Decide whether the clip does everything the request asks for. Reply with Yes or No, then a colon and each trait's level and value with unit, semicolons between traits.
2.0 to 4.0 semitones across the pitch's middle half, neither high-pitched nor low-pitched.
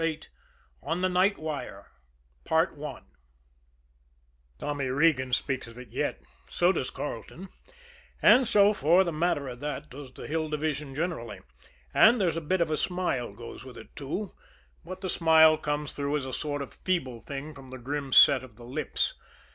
No: average, 4.6 semitones; medium, 145 Hz